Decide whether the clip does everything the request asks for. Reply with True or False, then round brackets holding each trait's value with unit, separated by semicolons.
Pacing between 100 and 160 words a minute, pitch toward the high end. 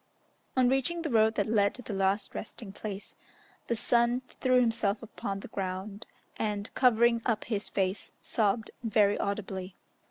True (155 wpm; 215 Hz)